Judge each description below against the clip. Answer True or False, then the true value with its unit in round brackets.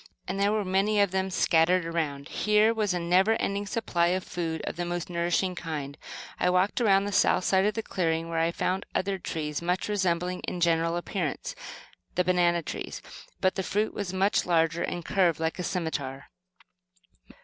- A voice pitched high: False (180 Hz)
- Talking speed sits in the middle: True (190 wpm)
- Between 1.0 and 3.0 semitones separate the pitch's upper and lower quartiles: True (2.6 semitones)